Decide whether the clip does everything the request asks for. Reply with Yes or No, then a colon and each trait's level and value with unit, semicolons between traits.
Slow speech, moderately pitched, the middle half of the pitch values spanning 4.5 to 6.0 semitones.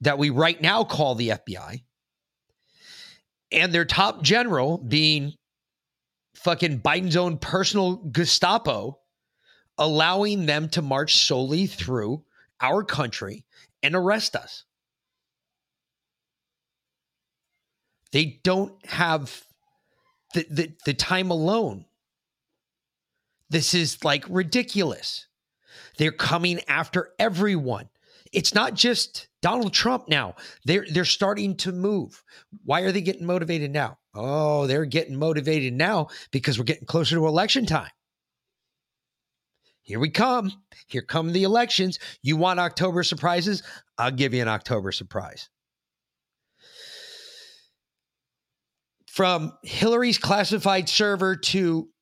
Yes: slow, 110 wpm; medium, 170 Hz; average, 4.9 semitones